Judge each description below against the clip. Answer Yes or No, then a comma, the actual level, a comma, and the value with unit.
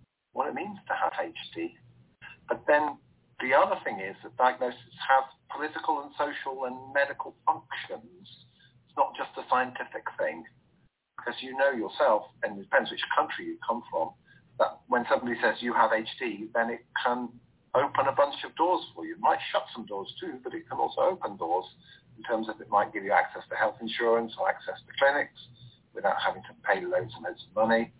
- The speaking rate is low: No, average, 195 wpm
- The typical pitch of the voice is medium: No, low, 125 Hz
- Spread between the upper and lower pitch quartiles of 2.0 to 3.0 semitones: No, average, 3.6 semitones